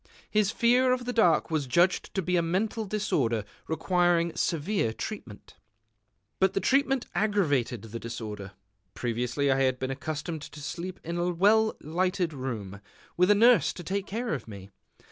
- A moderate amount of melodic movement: No, wide, 7.5 semitones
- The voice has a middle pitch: Yes, medium, 170 Hz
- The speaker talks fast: No, average, 165 wpm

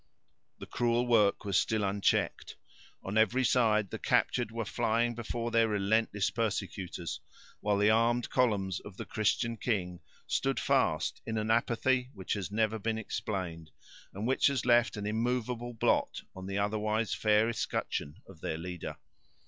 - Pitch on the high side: No, low, 110 Hz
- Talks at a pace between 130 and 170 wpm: Yes, average, 155 wpm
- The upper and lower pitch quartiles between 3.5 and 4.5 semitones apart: No, average, 2.8 semitones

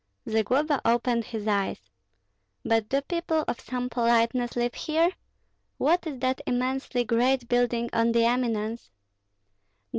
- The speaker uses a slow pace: Yes, slow, 125 wpm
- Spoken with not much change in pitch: Yes, narrow, 2.3 semitones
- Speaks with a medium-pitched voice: No, high, 245 Hz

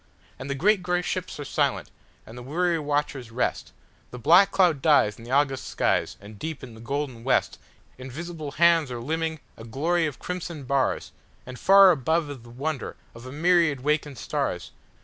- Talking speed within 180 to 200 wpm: No, average, 170 wpm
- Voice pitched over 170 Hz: No, medium, 145 Hz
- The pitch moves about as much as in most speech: Yes, average, 4.6 semitones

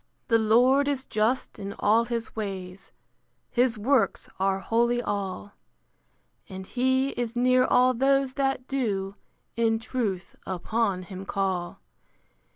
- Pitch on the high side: Yes, high, 230 Hz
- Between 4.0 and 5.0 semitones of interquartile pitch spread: Yes, average, 4.6 semitones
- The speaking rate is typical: No, slow, 125 wpm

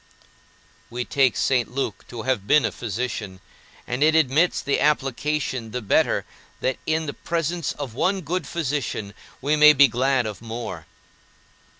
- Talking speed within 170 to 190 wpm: No, average, 155 wpm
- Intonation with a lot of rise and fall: No, average, 3.9 semitones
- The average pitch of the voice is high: No, low, 135 Hz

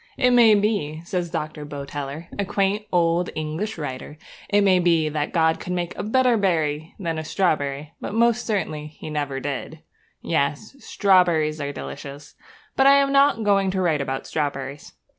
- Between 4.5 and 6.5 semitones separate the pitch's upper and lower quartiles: Yes, average, 5.2 semitones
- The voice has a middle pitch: Yes, medium, 165 Hz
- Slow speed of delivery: No, average, 170 wpm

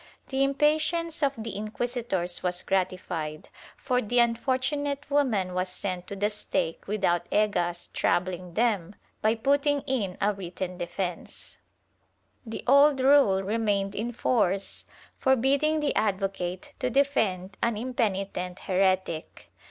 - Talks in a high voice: Yes, high, 210 Hz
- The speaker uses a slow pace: Yes, slow, 120 wpm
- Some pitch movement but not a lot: No, wide, 6.2 semitones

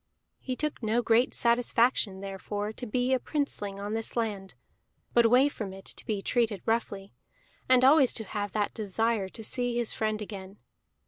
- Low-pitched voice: No, high, 225 Hz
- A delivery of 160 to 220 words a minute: Yes, average, 175 wpm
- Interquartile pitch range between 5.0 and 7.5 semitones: No, average, 3.2 semitones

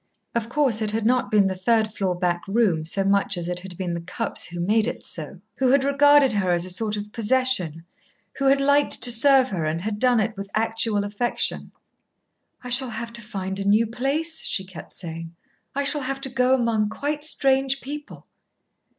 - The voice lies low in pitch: No, high, 220 Hz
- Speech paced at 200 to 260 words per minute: Yes, fast, 205 wpm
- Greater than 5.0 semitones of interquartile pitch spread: Yes, wide, 5.5 semitones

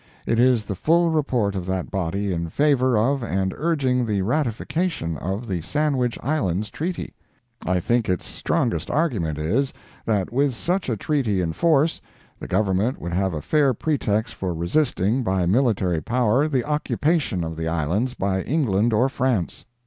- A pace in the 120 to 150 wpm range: No, average, 165 wpm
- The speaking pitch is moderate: No, low, 115 Hz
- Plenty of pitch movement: Yes, wide, 6.8 semitones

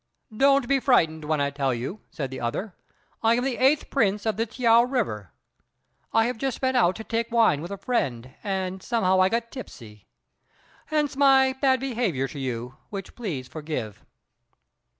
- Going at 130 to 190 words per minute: Yes, average, 175 wpm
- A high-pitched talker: Yes, high, 215 Hz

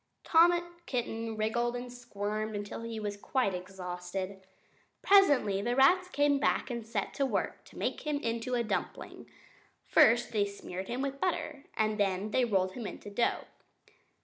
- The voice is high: Yes, high, 230 Hz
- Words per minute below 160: No, average, 165 wpm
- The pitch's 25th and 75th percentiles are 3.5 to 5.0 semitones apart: Yes, average, 4.7 semitones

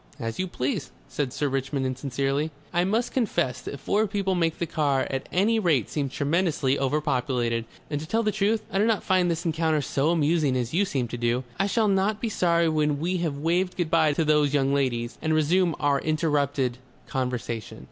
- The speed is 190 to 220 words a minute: Yes, average, 200 wpm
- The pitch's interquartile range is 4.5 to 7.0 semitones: Yes, average, 4.8 semitones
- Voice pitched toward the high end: No, medium, 155 Hz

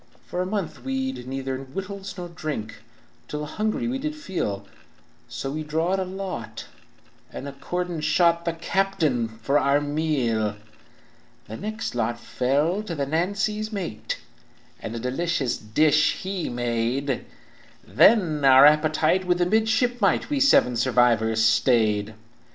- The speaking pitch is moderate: Yes, medium, 155 Hz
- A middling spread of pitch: No, wide, 7.3 semitones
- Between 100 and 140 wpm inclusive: Yes, slow, 135 wpm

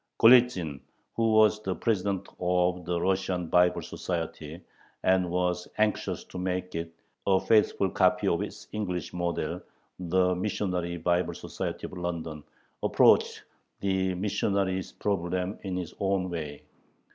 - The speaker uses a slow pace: Yes, slow, 130 wpm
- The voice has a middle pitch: No, very low, 90 Hz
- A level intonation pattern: Yes, narrow, 1.8 semitones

